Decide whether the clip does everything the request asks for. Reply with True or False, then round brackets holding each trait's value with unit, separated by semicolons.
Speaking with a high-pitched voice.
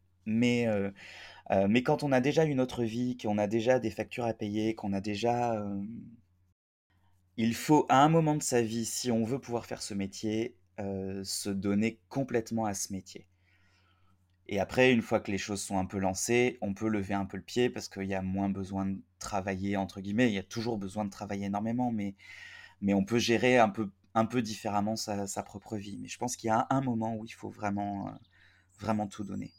False (105 Hz)